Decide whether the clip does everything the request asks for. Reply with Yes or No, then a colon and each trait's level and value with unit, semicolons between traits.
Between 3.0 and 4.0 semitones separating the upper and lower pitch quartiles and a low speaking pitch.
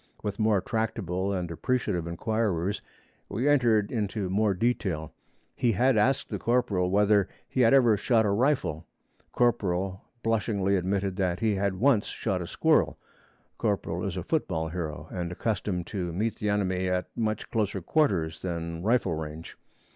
Yes: average, 3.7 semitones; low, 100 Hz